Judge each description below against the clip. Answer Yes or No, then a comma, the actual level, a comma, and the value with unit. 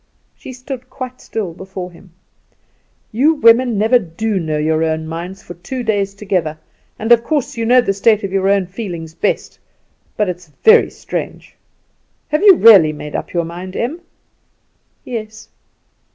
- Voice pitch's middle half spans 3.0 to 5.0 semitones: No, wide, 5.4 semitones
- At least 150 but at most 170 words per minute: Yes, average, 160 wpm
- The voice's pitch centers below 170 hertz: No, high, 200 Hz